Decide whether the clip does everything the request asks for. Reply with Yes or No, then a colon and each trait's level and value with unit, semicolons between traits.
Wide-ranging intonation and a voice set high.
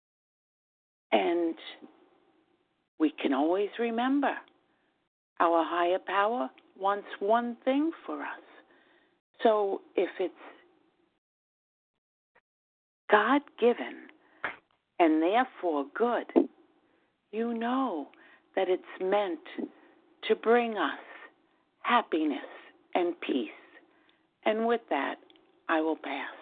Yes: wide, 8.0 semitones; very high, 280 Hz